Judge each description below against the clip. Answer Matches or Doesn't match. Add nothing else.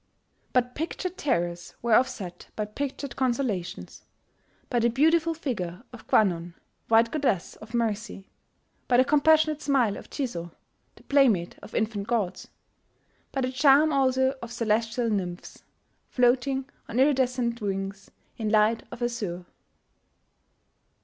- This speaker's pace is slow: Matches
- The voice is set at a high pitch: Matches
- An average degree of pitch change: Matches